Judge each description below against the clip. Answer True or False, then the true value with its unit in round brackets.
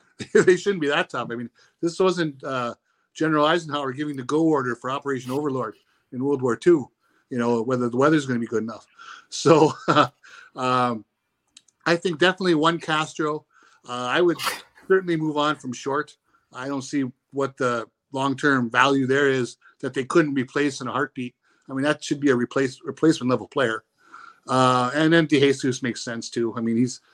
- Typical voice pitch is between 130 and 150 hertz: True (140 Hz)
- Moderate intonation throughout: True (3.7 semitones)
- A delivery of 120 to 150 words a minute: False (190 wpm)